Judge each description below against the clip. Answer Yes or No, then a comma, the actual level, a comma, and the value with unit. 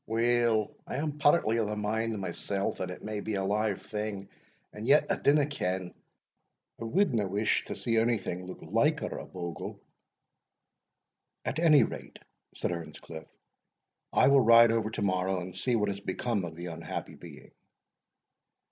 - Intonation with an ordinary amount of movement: Yes, average, 3.9 semitones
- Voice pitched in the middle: No, low, 105 Hz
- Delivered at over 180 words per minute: No, average, 165 wpm